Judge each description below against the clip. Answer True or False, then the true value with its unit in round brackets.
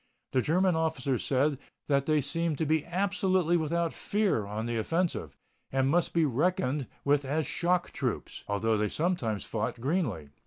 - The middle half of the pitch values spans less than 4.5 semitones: False (5.3 semitones)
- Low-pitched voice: False (150 Hz)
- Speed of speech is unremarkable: True (160 wpm)